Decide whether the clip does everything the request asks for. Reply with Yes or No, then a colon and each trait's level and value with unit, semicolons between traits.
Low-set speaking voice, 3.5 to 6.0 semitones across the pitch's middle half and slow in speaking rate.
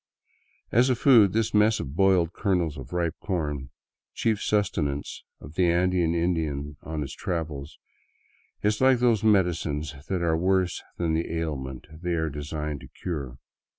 No: very low, 85 Hz; average, 4.3 semitones; average, 150 wpm